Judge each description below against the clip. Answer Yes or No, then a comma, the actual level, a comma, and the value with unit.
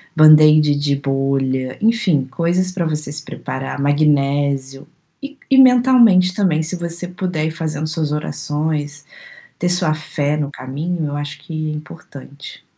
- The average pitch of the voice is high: No, medium, 155 Hz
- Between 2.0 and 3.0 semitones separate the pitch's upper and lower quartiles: No, average, 3.4 semitones